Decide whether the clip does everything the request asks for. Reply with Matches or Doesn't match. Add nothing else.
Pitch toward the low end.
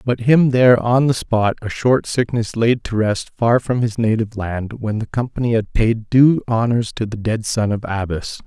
Matches